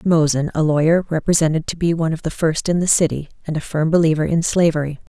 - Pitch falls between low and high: Yes, medium, 160 Hz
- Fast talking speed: Yes, fast, 220 wpm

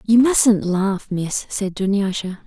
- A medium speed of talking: Yes, average, 145 wpm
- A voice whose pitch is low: No, high, 200 Hz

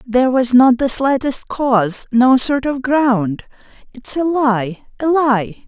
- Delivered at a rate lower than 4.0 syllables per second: Yes, 3.7 syllables/s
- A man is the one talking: No, female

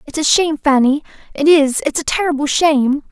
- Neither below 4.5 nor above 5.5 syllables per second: No, 5.9 syllables/s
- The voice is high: Yes, very high, 295 Hz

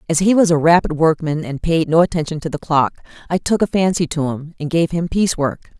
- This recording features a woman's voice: Yes, female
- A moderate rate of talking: No, fast, 250 wpm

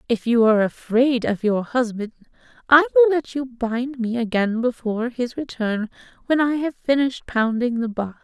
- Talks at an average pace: Yes, average, 175 wpm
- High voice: Yes, high, 240 Hz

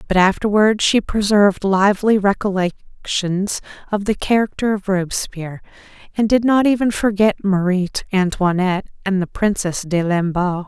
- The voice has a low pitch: No, high, 195 Hz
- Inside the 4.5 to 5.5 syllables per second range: Yes, 5.0 syllables/s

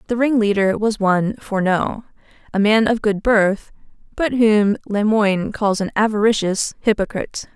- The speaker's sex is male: No, female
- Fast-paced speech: No, average, 145 wpm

